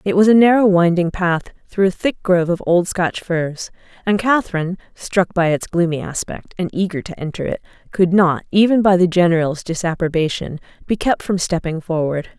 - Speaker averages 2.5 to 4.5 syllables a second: No, 5.2 syllables/s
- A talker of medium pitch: Yes, medium, 180 Hz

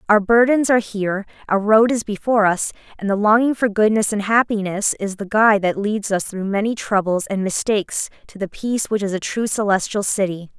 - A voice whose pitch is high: Yes, high, 205 Hz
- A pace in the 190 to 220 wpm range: Yes, fast, 205 wpm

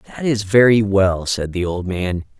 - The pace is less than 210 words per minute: Yes, average, 200 wpm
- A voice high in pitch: No, low, 100 Hz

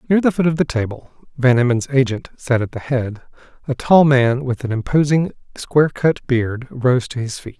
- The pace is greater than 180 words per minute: Yes, average, 190 wpm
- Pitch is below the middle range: Yes, low, 130 Hz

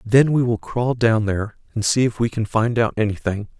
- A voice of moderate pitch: No, low, 115 Hz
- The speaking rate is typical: No, fast, 235 wpm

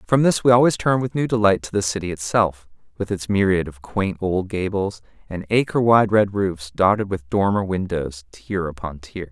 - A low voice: Yes, very low, 95 Hz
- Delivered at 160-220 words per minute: Yes, average, 200 wpm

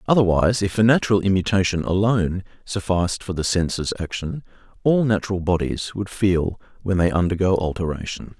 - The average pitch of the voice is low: Yes, very low, 95 Hz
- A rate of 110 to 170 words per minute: Yes, average, 145 wpm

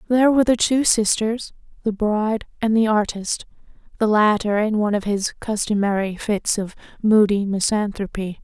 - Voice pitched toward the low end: No, high, 215 Hz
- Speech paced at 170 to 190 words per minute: No, average, 140 wpm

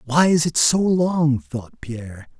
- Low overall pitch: No, medium, 145 Hz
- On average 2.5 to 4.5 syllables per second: Yes, 3.9 syllables/s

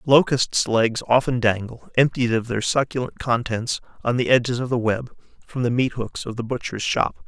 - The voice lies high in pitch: No, low, 120 Hz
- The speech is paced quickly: No, average, 190 wpm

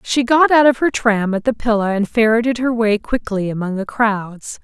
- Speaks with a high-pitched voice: Yes, high, 225 Hz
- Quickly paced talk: Yes, fast, 220 wpm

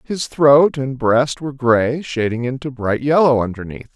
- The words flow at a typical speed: Yes, average, 165 wpm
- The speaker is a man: Yes, male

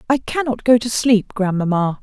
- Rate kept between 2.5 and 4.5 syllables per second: Yes, 4.4 syllables/s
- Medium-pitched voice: No, high, 225 Hz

